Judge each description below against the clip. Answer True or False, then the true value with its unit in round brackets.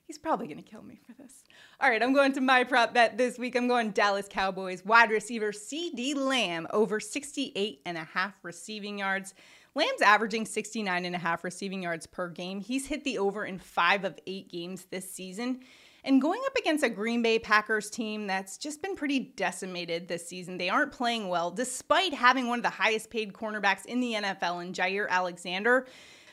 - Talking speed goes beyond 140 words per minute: True (200 wpm)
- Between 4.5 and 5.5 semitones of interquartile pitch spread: True (5.1 semitones)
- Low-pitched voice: False (215 Hz)